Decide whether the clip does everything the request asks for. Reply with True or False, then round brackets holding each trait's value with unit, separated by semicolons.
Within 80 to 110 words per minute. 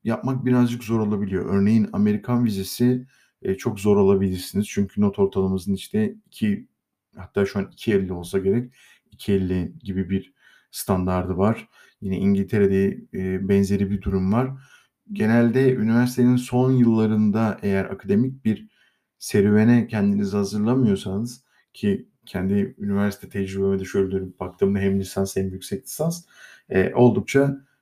False (125 wpm)